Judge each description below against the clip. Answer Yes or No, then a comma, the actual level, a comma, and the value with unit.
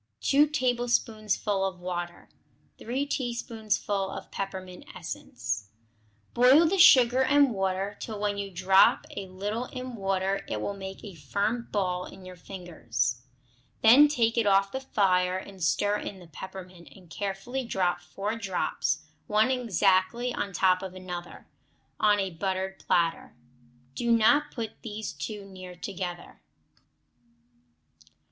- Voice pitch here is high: Yes, high, 195 Hz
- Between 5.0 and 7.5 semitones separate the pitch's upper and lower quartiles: No, average, 3.9 semitones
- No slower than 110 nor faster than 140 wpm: Yes, slow, 135 wpm